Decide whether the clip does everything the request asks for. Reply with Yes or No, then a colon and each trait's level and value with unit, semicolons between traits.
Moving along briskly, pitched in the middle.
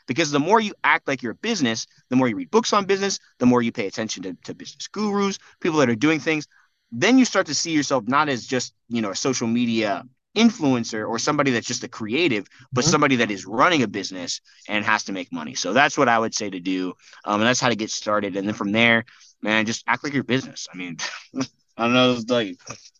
No: fast, 245 wpm; low, 125 Hz